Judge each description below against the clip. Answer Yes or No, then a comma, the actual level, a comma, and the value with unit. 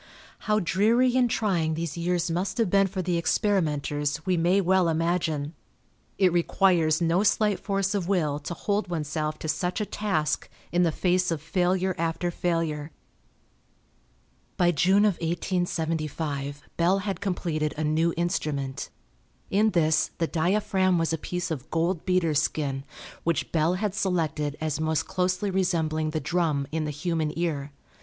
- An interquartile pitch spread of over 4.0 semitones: No, average, 3.2 semitones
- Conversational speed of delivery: Yes, average, 155 wpm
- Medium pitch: Yes, medium, 170 Hz